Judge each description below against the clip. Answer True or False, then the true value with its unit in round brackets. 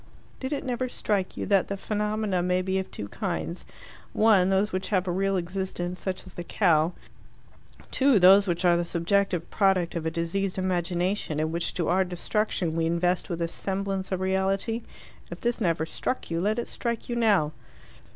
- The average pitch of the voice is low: False (185 Hz)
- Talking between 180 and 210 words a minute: True (185 wpm)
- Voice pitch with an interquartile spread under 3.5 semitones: True (2.6 semitones)